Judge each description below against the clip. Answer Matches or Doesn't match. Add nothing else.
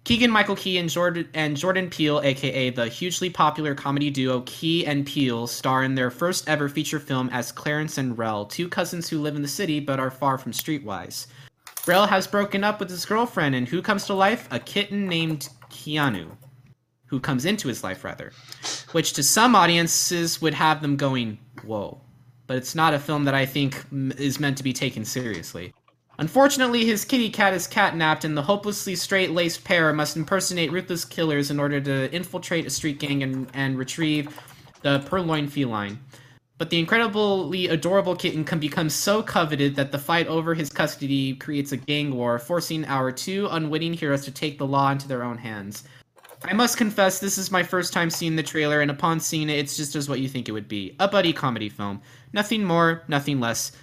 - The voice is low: Doesn't match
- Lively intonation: Doesn't match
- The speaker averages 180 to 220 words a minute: Matches